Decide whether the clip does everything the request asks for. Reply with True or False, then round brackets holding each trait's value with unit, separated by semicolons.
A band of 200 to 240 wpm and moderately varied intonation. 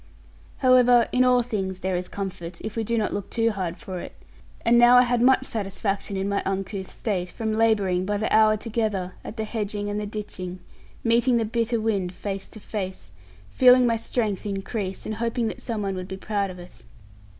True (205 wpm; 3.2 semitones)